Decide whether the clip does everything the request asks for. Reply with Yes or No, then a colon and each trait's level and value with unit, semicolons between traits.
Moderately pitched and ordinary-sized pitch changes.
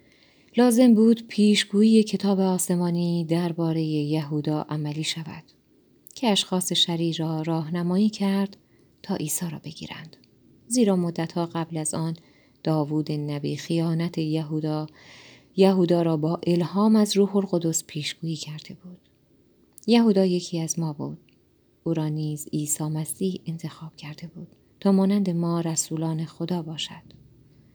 Yes: medium, 165 Hz; average, 3.4 semitones